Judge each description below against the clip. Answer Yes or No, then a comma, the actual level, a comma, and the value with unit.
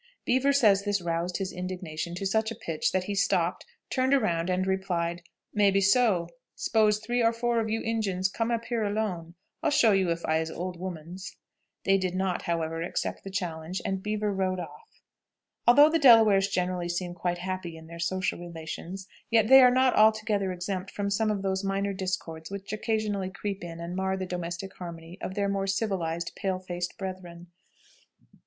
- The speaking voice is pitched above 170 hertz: Yes, high, 190 Hz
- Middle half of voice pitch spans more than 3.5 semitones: No, average, 3.2 semitones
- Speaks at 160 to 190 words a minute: Yes, average, 185 wpm